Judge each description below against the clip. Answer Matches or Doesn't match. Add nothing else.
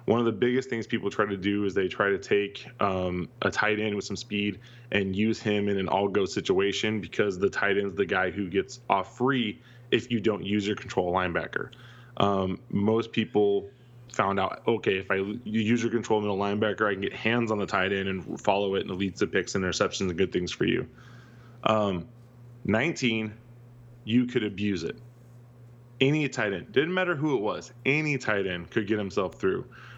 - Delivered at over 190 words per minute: Matches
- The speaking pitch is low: Matches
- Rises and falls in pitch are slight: Doesn't match